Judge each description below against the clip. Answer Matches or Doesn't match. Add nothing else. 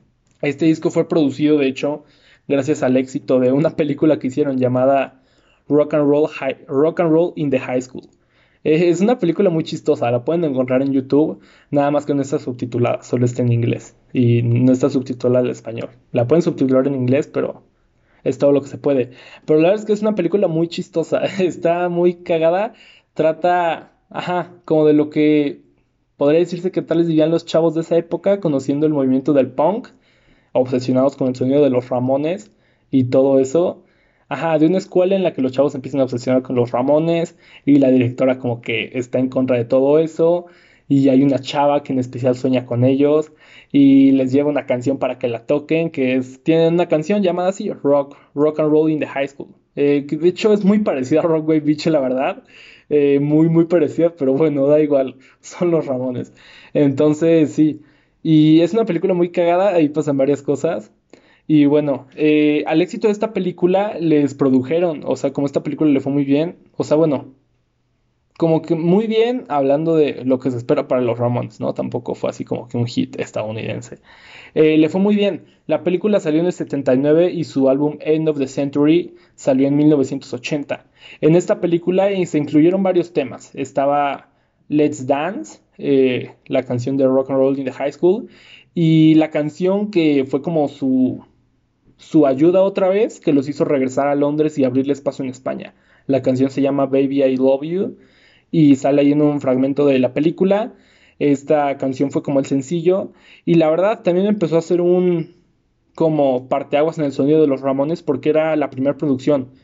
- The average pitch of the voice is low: Doesn't match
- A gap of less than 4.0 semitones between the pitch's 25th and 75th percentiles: Matches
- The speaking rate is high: Matches